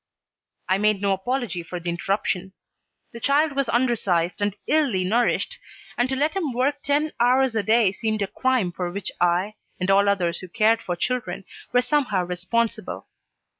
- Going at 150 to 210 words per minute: Yes, average, 170 wpm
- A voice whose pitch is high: Yes, high, 215 Hz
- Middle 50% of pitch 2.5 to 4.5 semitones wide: No, average, 5.3 semitones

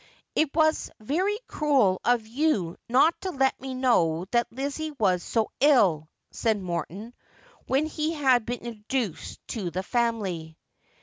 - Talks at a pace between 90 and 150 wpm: Yes, average, 145 wpm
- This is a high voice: Yes, high, 240 Hz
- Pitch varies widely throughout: Yes, wide, 6.7 semitones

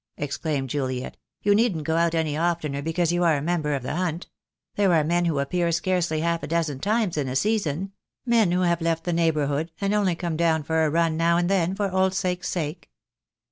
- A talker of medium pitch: Yes, medium, 170 Hz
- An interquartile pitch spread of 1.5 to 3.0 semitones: Yes, average, 2.7 semitones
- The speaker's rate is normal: No, fast, 225 wpm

